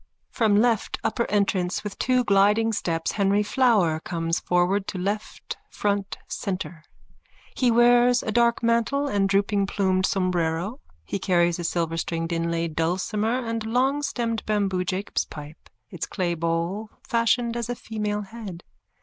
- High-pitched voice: Yes, high, 200 Hz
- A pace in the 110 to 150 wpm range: Yes, average, 140 wpm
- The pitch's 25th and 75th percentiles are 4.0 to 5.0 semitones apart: Yes, average, 4.5 semitones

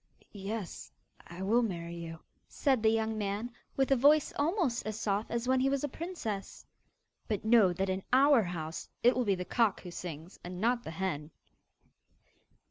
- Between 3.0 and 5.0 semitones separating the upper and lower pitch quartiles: No, wide, 5.5 semitones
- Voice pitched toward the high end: Yes, high, 215 Hz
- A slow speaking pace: No, average, 180 wpm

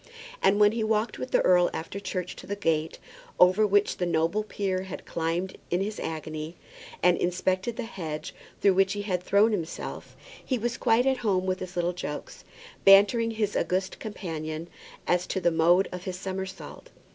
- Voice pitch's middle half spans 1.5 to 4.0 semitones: Yes, average, 2.9 semitones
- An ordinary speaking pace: Yes, average, 180 wpm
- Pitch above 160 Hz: Yes, medium, 185 Hz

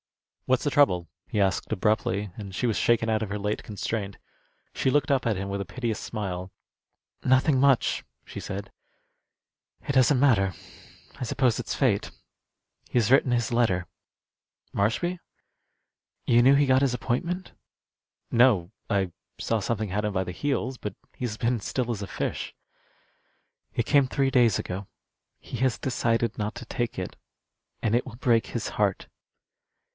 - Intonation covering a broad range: No, average, 4.1 semitones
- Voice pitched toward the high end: No, low, 115 Hz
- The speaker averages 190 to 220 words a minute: No, average, 160 wpm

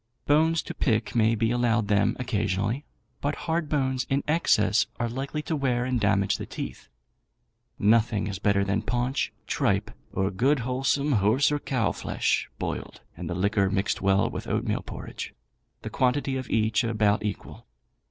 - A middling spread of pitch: Yes, average, 4.7 semitones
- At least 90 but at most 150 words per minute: No, average, 160 wpm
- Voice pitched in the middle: No, low, 115 Hz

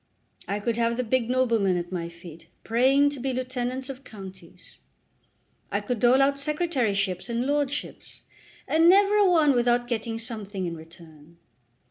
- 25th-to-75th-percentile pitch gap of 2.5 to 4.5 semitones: No, wide, 5.5 semitones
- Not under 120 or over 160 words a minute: Yes, average, 155 wpm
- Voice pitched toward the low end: No, high, 240 Hz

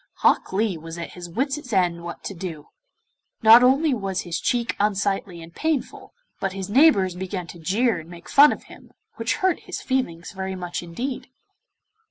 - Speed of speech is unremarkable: Yes, average, 180 wpm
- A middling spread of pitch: No, wide, 5.9 semitones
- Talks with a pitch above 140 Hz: Yes, high, 190 Hz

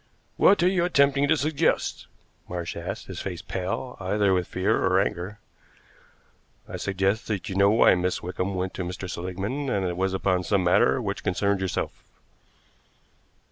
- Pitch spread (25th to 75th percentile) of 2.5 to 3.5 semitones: No, average, 4.5 semitones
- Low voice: Yes, very low, 95 Hz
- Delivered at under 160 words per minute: No, average, 170 wpm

